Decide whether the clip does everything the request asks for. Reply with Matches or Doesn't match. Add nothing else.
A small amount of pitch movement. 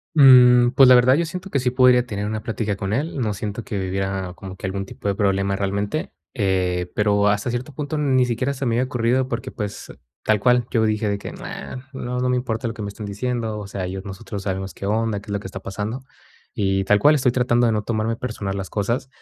Doesn't match